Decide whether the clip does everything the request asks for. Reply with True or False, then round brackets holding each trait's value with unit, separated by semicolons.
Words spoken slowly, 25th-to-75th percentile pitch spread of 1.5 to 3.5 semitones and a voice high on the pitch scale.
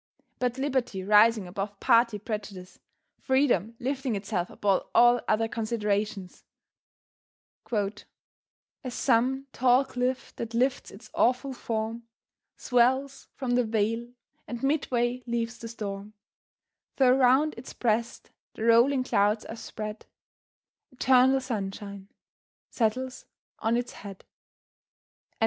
True (110 wpm; 3.2 semitones; 235 Hz)